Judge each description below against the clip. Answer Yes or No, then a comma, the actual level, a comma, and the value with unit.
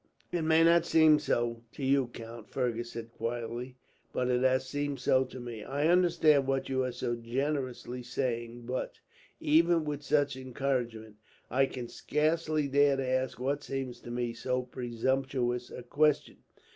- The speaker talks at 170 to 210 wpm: No, average, 160 wpm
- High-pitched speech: No, low, 130 Hz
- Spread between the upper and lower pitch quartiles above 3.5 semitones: No, average, 3.0 semitones